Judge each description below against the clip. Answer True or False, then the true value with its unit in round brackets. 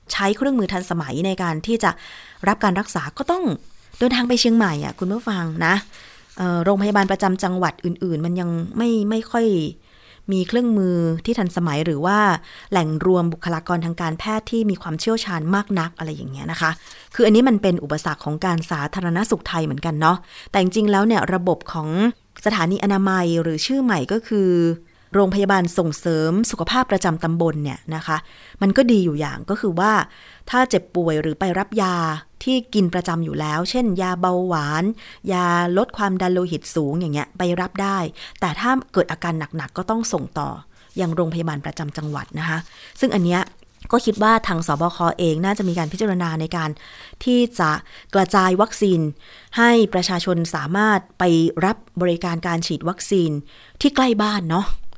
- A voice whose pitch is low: False (180 Hz)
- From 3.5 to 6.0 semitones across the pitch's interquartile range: True (3.9 semitones)